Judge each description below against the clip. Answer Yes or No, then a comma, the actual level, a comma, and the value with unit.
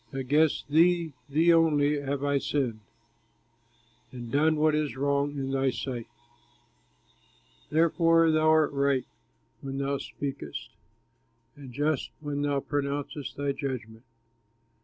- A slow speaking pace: Yes, slow, 115 wpm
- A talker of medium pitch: Yes, medium, 145 Hz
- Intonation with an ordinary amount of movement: No, narrow, 2.2 semitones